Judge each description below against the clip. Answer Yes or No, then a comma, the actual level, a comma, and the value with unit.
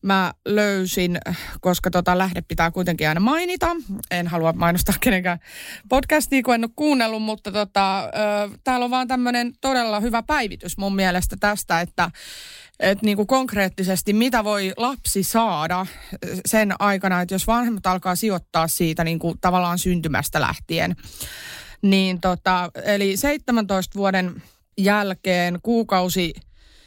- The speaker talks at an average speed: Yes, average, 135 wpm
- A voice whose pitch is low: No, high, 195 Hz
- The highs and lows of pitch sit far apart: No, average, 4.0 semitones